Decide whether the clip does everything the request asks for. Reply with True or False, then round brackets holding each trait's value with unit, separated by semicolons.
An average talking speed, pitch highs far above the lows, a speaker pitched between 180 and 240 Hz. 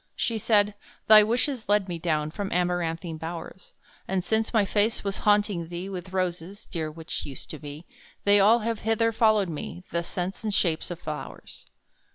False (180 wpm; 3.9 semitones; 190 Hz)